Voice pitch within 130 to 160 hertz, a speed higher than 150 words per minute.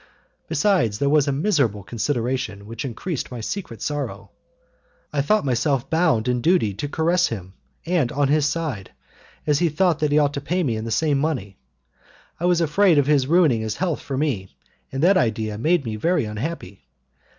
Yes: medium, 140 Hz; average, 185 wpm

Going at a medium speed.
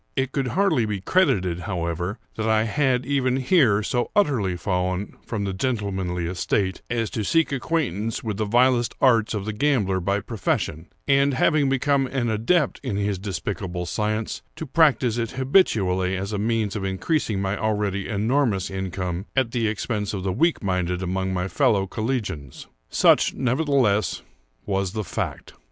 Yes: average, 160 wpm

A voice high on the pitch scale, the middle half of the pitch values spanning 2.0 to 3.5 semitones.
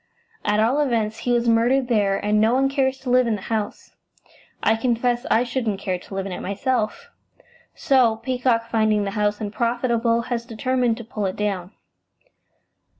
Yes: high, 230 Hz; average, 2.8 semitones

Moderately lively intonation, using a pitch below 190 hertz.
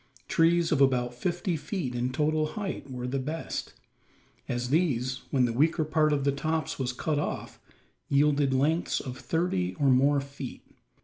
Yes: average, 3.6 semitones; medium, 140 Hz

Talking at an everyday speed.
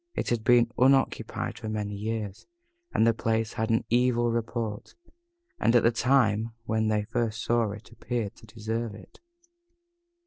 Yes: average, 160 wpm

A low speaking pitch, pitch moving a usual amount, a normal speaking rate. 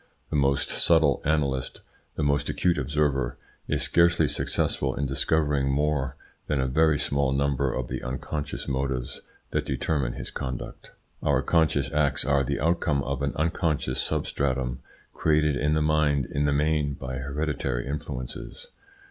No: very low, 70 Hz; narrow, 2.2 semitones; average, 150 wpm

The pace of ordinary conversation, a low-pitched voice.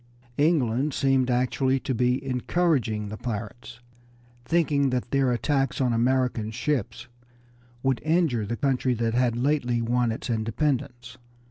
No: slow, 130 wpm; low, 125 Hz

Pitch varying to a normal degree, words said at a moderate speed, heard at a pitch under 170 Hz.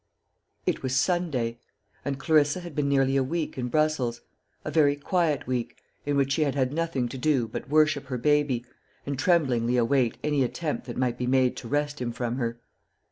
Yes: average, 3.2 semitones; average, 190 wpm; medium, 140 Hz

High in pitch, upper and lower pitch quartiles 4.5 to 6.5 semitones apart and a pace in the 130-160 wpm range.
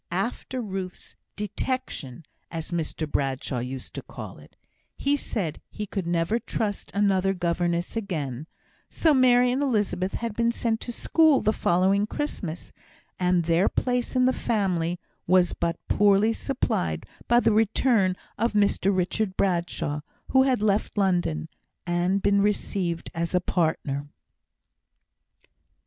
Yes: high, 195 Hz; average, 4.8 semitones; slow, 135 wpm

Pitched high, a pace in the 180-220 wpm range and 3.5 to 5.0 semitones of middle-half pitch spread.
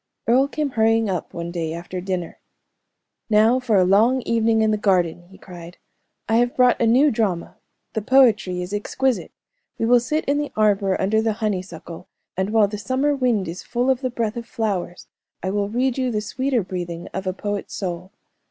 Yes: high, 215 Hz; average, 195 wpm; average, 4.6 semitones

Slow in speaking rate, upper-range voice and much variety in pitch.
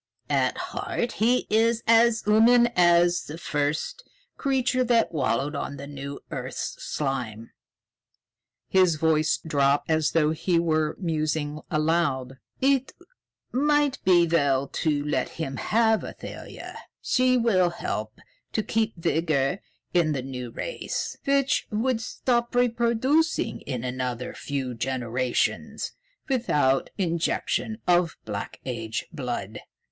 No: slow, 120 wpm; medium, 165 Hz; wide, 8.5 semitones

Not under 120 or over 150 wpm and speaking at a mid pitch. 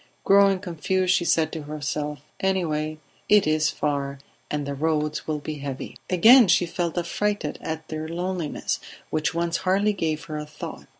No: average, 165 wpm; medium, 160 Hz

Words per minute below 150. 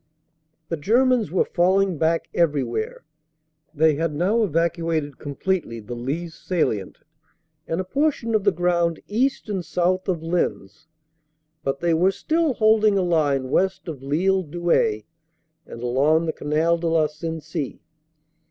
Yes: average, 140 wpm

